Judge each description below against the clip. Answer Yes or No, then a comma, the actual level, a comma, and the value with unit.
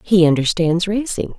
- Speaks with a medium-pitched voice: Yes, medium, 180 Hz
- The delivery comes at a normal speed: No, slow, 130 wpm